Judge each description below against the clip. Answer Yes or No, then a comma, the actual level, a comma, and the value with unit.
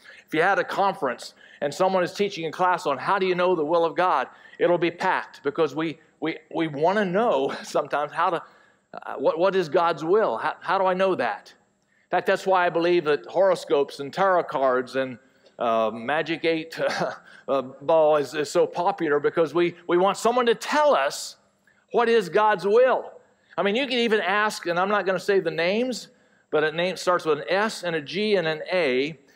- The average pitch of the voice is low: No, medium, 175 Hz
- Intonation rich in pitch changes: No, average, 4.1 semitones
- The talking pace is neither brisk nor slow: No, fast, 215 wpm